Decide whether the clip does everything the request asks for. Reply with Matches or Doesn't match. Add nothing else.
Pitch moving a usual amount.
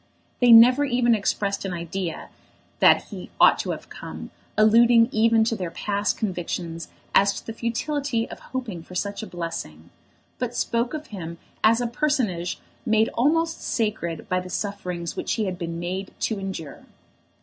Matches